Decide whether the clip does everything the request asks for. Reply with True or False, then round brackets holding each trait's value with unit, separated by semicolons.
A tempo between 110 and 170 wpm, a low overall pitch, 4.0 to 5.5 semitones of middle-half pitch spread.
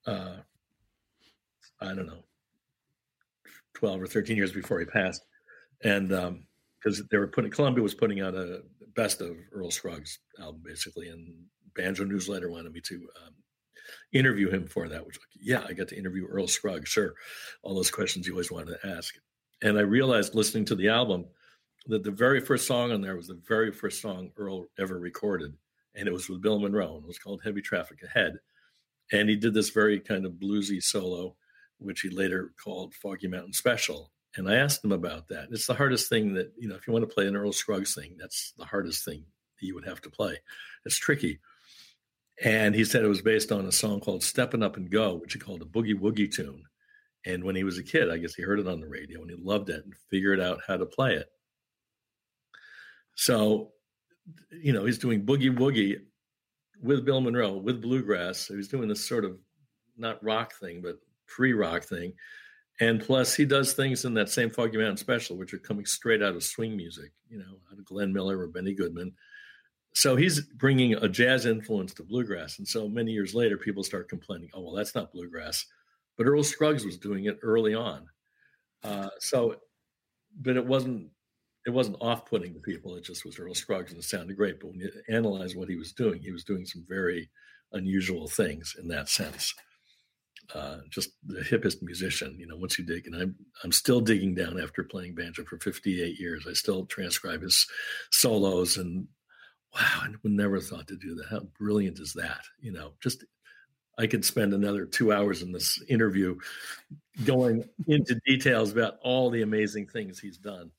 False (200 wpm; 105 Hz; 4.6 semitones)